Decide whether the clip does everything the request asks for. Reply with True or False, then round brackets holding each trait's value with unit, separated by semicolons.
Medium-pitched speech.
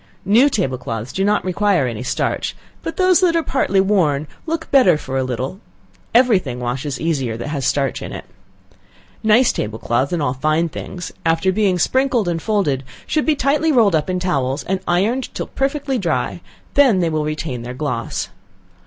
True (175 Hz)